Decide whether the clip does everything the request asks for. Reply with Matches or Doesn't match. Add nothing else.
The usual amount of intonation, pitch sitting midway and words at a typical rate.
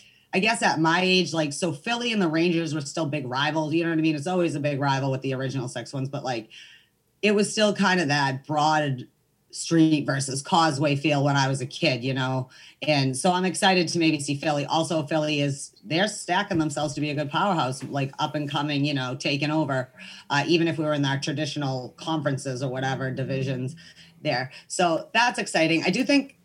Doesn't match